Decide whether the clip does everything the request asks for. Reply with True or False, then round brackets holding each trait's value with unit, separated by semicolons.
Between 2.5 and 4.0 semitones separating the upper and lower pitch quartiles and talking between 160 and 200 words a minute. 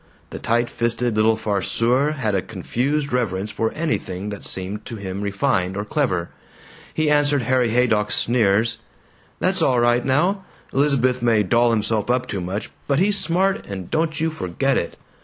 False (5.2 semitones; 165 wpm)